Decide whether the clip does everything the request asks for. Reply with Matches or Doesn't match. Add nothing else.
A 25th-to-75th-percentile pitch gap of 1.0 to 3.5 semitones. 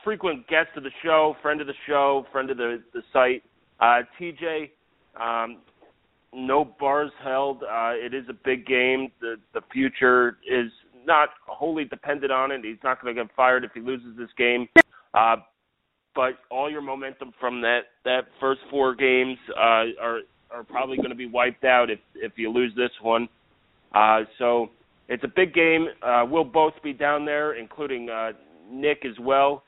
Matches